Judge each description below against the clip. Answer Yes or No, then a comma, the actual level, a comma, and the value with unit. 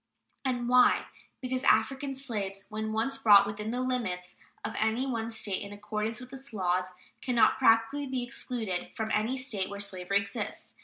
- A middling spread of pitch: Yes, average, 3.9 semitones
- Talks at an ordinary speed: Yes, average, 170 wpm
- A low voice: No, high, 225 Hz